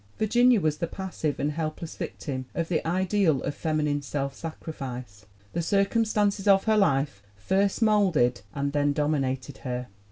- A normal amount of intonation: No, wide, 5.9 semitones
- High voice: No, medium, 155 Hz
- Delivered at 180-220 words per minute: No, average, 150 wpm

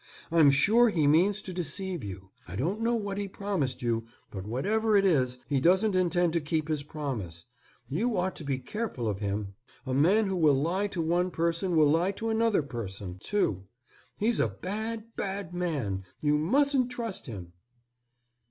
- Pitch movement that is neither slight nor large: No, wide, 7.5 semitones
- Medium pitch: Yes, medium, 170 Hz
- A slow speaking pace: No, average, 180 wpm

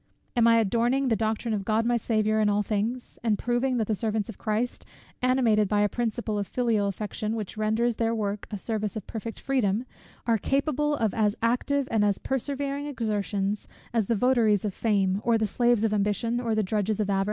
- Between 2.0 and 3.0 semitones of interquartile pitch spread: Yes, narrow, 2.5 semitones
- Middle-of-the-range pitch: No, high, 220 Hz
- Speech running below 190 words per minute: No, fast, 205 wpm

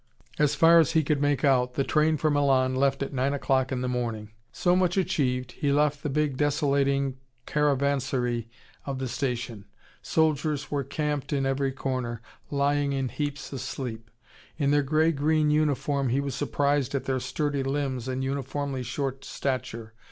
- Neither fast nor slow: Yes, average, 165 wpm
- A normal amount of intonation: No, narrow, 2.1 semitones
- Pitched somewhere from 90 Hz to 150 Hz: Yes, medium, 140 Hz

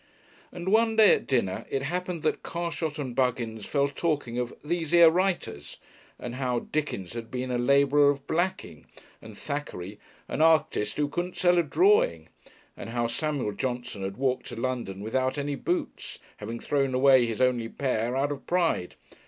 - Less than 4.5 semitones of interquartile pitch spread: No, average, 5.2 semitones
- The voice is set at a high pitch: No, low, 135 Hz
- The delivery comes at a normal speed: Yes, average, 170 wpm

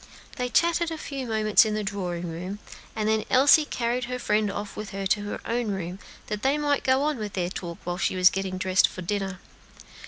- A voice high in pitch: Yes, high, 210 Hz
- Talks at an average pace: No, fast, 220 wpm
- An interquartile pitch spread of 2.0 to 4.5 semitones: No, average, 4.9 semitones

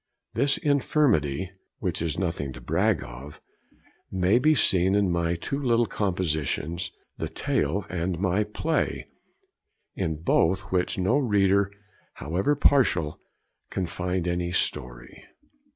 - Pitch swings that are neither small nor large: Yes, average, 3.9 semitones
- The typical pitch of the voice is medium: No, very low, 90 Hz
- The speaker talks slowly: Yes, slow, 120 wpm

